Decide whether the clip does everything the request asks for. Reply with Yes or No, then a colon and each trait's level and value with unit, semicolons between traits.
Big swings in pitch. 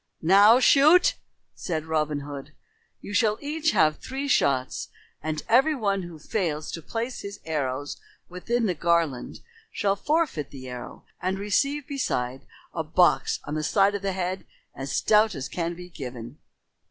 Yes: wide, 6.7 semitones